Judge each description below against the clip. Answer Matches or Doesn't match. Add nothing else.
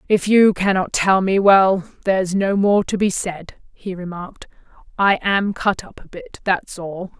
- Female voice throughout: Matches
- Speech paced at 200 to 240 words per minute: Doesn't match